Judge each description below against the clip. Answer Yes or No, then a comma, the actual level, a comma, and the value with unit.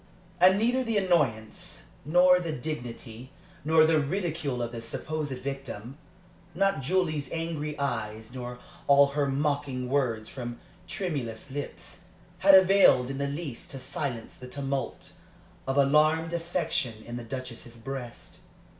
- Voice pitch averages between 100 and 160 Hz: Yes, medium, 140 Hz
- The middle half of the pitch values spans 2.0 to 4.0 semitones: No, average, 4.6 semitones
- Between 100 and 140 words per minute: Yes, slow, 135 wpm